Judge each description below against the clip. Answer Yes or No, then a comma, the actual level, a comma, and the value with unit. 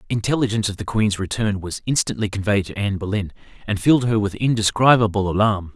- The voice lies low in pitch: Yes, low, 105 Hz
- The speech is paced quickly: No, average, 175 wpm